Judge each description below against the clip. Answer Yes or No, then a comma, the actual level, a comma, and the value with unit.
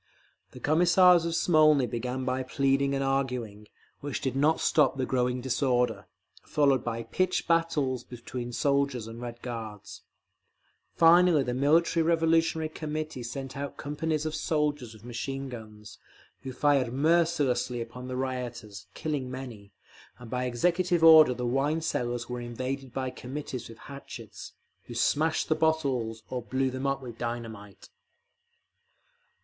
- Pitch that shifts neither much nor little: Yes, average, 4.0 semitones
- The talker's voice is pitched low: Yes, low, 130 Hz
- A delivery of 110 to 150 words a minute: Yes, average, 140 wpm